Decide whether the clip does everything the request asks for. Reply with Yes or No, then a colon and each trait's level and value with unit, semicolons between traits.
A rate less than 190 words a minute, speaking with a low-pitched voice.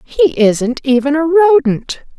No: slow, 135 wpm; very high, 285 Hz